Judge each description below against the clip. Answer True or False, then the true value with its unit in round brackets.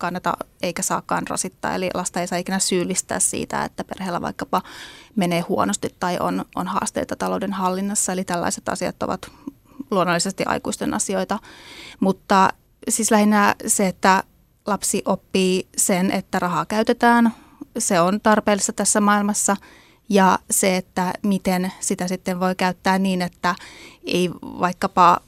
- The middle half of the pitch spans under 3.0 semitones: True (2.5 semitones)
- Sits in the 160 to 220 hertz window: True (190 Hz)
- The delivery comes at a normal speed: True (135 wpm)